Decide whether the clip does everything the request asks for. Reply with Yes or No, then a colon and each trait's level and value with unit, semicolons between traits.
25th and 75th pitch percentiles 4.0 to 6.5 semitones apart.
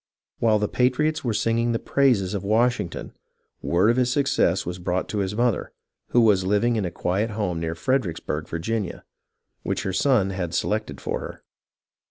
Yes: average, 4.5 semitones